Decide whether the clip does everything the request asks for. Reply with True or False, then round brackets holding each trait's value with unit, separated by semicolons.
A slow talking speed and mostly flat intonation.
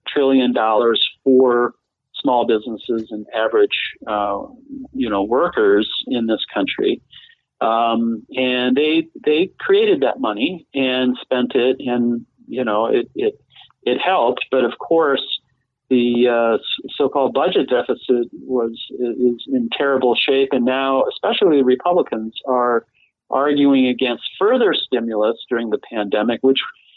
False (125 wpm; 4.1 semitones)